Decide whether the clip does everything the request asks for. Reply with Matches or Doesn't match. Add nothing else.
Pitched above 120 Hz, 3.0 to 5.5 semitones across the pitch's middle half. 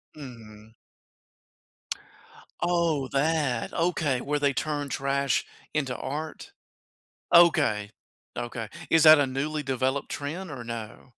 Matches